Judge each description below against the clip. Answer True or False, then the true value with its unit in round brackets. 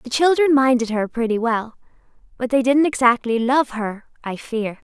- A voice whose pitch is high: True (245 Hz)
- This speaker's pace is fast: False (170 wpm)